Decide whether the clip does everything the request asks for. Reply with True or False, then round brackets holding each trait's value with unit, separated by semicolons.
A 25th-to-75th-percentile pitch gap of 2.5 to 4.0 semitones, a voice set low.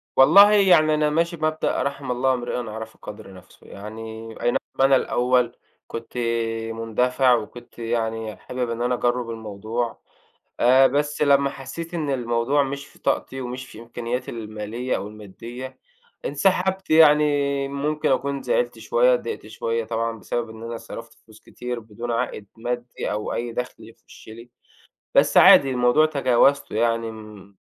True (3.5 semitones; 125 Hz)